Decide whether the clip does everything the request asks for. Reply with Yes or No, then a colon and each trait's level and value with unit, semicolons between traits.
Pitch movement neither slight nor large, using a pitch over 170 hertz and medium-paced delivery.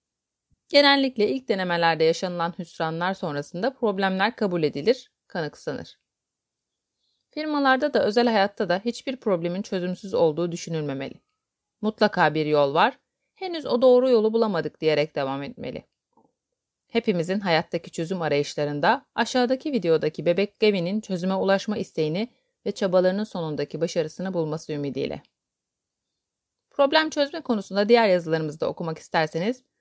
No: wide, 6.2 semitones; high, 190 Hz; average, 115 wpm